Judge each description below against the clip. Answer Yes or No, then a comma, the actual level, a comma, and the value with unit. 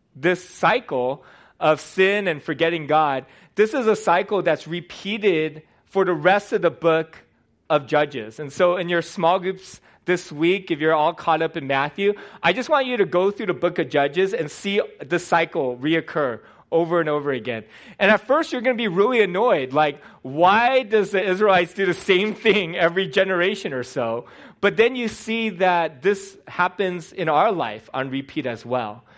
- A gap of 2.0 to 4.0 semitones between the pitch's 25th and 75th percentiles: No, average, 4.4 semitones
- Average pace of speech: Yes, average, 190 wpm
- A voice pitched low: No, medium, 175 Hz